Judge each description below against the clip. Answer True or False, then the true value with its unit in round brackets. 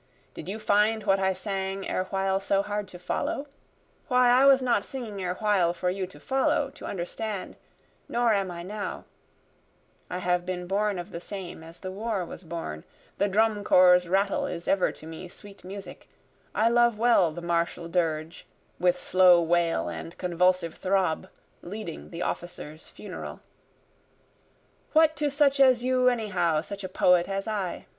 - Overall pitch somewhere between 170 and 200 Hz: True (190 Hz)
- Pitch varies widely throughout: False (3.4 semitones)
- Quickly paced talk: False (165 wpm)